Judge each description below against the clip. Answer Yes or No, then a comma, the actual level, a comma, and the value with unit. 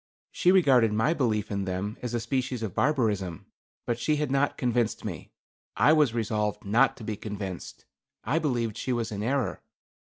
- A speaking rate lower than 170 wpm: No, average, 180 wpm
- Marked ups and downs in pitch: No, average, 4.2 semitones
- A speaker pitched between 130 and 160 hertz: No, low, 115 Hz